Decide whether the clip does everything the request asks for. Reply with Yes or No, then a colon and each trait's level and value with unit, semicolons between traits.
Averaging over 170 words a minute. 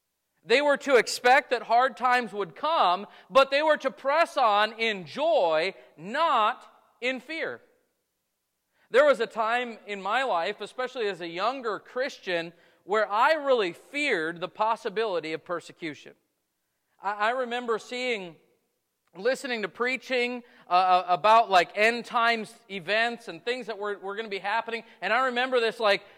No: average, 155 wpm